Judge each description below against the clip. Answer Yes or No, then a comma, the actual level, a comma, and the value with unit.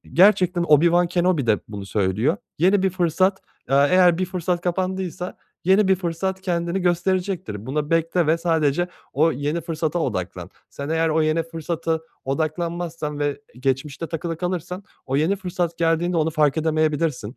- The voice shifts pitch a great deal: No, average, 3.0 semitones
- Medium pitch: Yes, medium, 165 Hz